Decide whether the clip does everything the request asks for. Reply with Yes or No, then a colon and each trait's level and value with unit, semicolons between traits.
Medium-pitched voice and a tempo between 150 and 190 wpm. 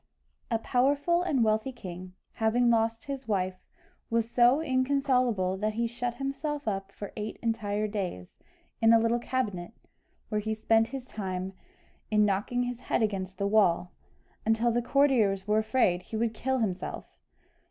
No: high, 225 Hz; average, 155 wpm